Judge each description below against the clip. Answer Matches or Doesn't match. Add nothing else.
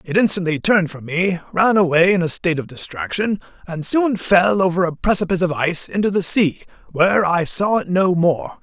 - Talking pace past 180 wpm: Matches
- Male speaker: Matches